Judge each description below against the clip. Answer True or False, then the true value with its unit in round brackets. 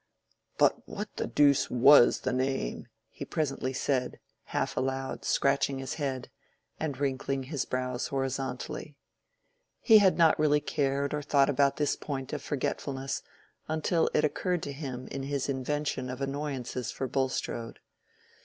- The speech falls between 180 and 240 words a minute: False (145 wpm)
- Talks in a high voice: False (135 Hz)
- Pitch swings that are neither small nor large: False (1.9 semitones)